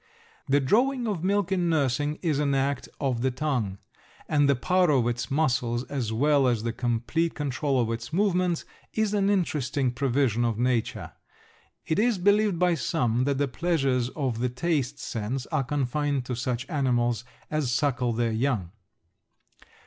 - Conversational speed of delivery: Yes, average, 165 wpm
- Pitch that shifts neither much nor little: Yes, average, 4.7 semitones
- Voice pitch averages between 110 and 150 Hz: Yes, low, 135 Hz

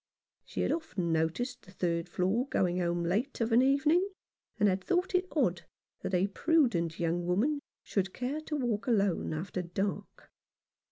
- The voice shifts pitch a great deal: Yes, wide, 7.5 semitones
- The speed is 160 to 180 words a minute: Yes, average, 165 wpm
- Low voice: No, high, 200 Hz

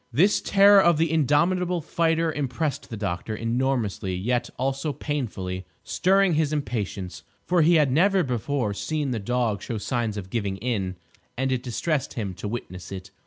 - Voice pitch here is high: No, low, 130 Hz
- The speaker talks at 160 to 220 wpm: Yes, average, 165 wpm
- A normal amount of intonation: No, wide, 7.1 semitones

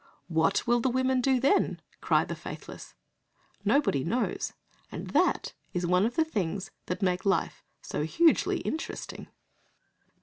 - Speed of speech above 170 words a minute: No, average, 140 wpm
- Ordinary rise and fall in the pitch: No, wide, 6.5 semitones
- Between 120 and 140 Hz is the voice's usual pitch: No, high, 220 Hz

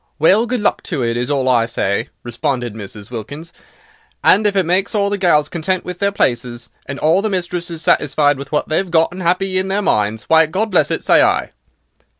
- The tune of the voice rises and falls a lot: Yes, wide, 7.0 semitones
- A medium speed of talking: No, fast, 210 wpm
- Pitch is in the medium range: Yes, medium, 160 Hz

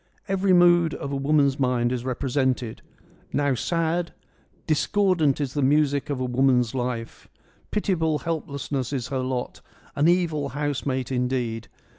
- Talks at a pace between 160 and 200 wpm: No, average, 145 wpm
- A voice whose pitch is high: No, medium, 140 Hz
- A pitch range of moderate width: Yes, average, 3.8 semitones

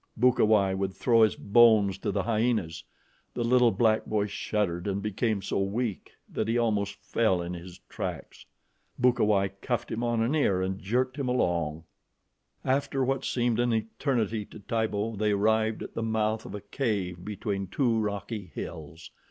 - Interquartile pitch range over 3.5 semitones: No, average, 3.1 semitones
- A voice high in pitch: No, low, 110 Hz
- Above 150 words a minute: Yes, average, 165 wpm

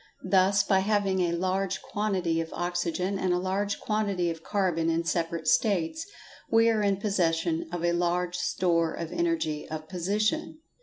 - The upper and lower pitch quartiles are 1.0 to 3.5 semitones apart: Yes, average, 3.0 semitones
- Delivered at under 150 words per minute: No, average, 160 wpm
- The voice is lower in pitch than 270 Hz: Yes, medium, 185 Hz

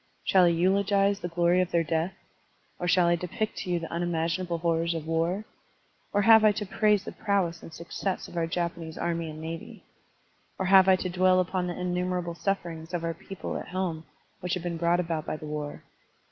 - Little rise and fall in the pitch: Yes, narrow, 2.0 semitones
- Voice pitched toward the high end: No, medium, 175 Hz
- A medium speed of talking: No, fast, 210 wpm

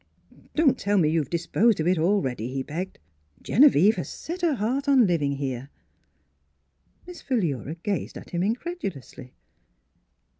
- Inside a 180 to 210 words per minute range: No, average, 160 wpm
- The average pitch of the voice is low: No, medium, 185 Hz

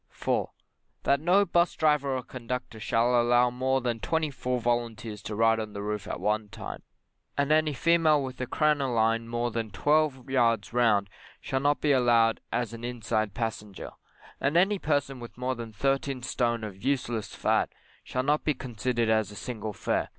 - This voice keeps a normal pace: Yes, average, 180 wpm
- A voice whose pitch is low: Yes, low, 120 Hz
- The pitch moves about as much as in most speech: Yes, average, 3.6 semitones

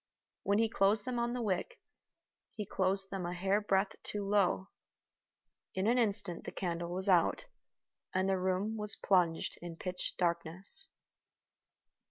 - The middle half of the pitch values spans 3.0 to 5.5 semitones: No, narrow, 2.5 semitones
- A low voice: No, high, 195 Hz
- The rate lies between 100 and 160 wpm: Yes, average, 150 wpm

